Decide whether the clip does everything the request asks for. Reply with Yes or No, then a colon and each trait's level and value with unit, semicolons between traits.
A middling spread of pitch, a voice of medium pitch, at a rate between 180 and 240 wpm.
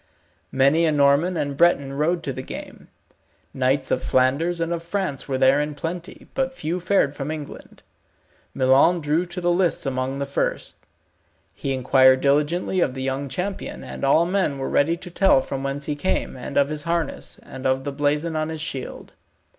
Yes: average, 3.9 semitones; medium, 145 Hz; average, 185 wpm